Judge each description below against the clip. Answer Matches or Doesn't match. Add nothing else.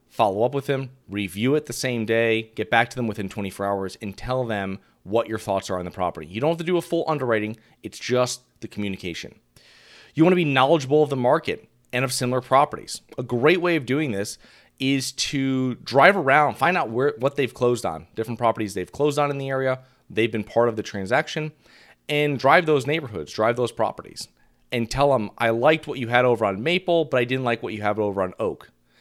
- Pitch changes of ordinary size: Matches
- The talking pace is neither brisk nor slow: Doesn't match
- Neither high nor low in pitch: Doesn't match